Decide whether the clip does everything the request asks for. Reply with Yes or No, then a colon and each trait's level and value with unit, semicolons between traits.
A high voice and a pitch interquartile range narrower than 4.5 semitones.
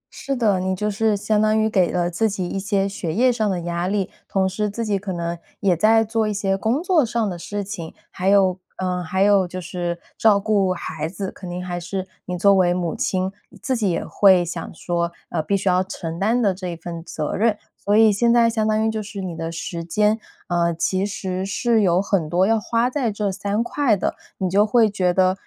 Yes: high, 195 Hz; average, 3.2 semitones